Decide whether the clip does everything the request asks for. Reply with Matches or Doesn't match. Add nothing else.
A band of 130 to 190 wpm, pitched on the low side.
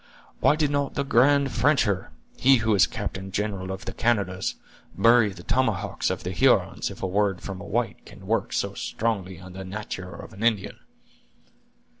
Matches